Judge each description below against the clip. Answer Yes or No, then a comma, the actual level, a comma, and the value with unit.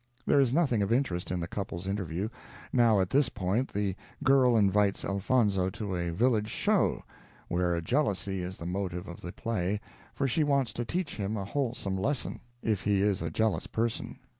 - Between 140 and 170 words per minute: No, average, 185 wpm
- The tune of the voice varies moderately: Yes, average, 4.4 semitones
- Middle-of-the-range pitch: No, low, 105 Hz